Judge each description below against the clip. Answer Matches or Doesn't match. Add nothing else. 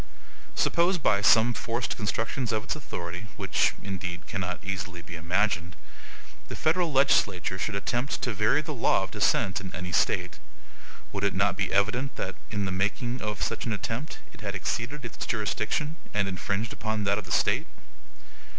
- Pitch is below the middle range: Matches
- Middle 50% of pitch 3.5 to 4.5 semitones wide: Matches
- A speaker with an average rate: Matches